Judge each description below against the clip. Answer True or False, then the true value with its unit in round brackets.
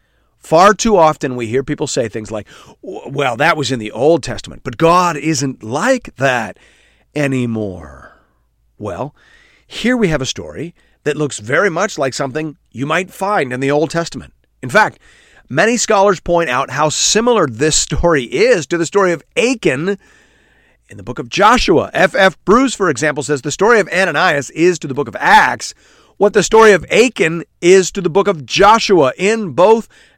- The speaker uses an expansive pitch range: True (6.1 semitones)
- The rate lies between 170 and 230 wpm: True (180 wpm)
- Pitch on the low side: False (165 Hz)